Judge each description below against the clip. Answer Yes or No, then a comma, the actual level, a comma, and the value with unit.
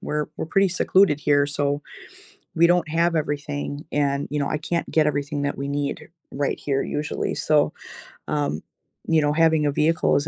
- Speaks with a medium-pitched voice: Yes, medium, 150 Hz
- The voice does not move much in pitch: Yes, narrow, 1.9 semitones